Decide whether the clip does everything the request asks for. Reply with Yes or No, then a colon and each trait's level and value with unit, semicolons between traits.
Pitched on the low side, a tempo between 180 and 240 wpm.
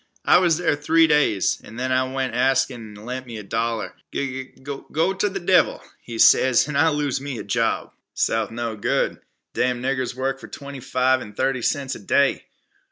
Yes: low, 130 Hz; fast, 205 wpm